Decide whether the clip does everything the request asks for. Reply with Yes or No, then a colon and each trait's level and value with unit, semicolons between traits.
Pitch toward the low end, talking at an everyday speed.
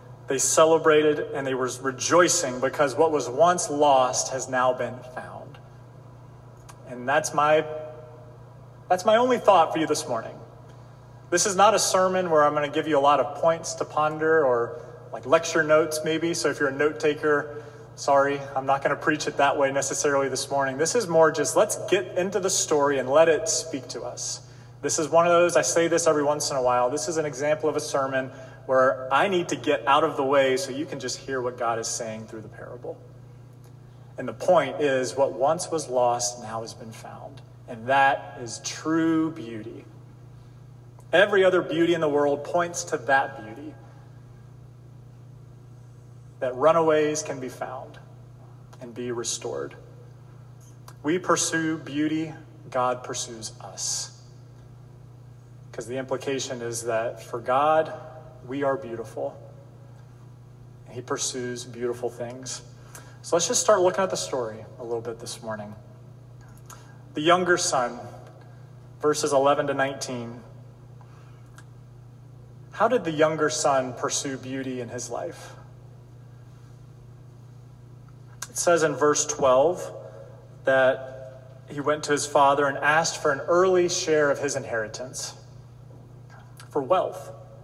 Yes: low, 130 Hz; average, 155 wpm